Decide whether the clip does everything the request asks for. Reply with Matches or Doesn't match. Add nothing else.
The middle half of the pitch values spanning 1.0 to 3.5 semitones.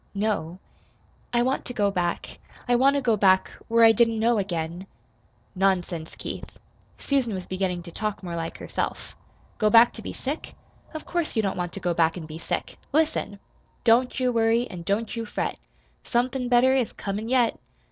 Doesn't match